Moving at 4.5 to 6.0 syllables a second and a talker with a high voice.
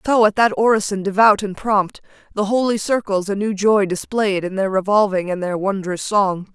Yes: 5.0 syllables/s; high, 200 Hz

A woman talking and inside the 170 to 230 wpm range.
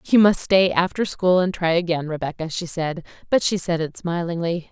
Yes: female; fast, 205 wpm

